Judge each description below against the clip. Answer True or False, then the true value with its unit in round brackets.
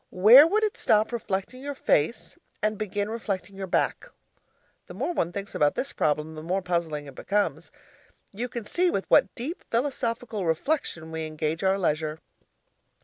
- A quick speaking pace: False (165 wpm)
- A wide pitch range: True (6.6 semitones)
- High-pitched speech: True (195 Hz)